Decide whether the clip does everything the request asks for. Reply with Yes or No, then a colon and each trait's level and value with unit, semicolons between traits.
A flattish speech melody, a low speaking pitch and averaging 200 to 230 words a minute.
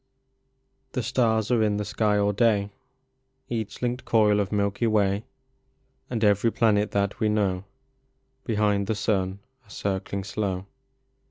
No: narrow, 1.8 semitones; low, 105 Hz; average, 140 wpm